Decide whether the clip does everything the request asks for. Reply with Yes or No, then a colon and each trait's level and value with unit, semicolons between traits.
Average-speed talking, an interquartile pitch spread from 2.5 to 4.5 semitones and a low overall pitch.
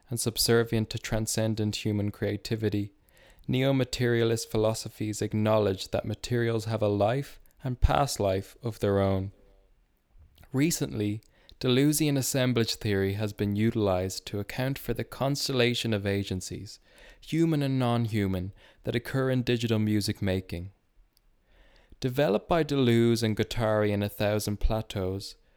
No: slow, 125 wpm; average, 3.1 semitones; low, 110 Hz